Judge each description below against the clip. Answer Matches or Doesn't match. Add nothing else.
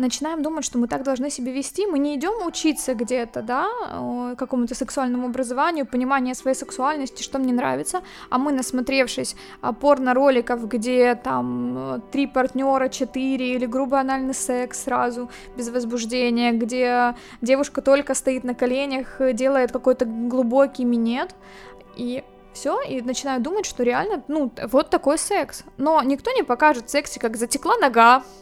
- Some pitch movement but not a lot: Doesn't match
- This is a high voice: Matches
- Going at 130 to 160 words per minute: Matches